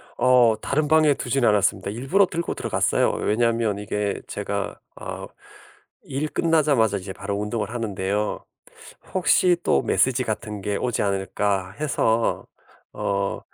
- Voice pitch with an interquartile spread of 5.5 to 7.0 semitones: No, average, 5.1 semitones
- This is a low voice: Yes, low, 115 Hz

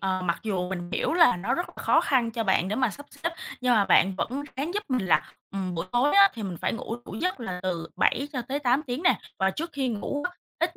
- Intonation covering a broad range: Yes, wide, 6.9 semitones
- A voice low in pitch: No, high, 240 Hz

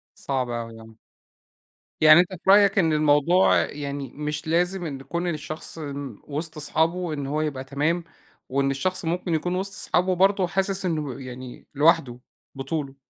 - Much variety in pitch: No, average, 4.3 semitones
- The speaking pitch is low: No, medium, 155 Hz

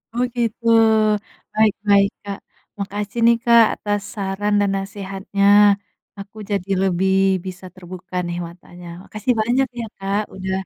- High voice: Yes, high, 200 Hz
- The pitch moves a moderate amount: No, narrow, 1.9 semitones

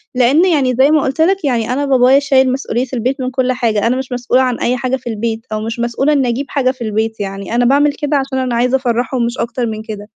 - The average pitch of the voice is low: No, very high, 250 Hz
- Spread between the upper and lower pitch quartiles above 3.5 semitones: No, narrow, 2.4 semitones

